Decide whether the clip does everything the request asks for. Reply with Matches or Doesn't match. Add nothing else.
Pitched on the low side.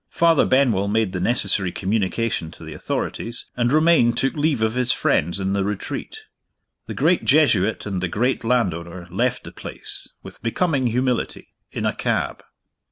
Matches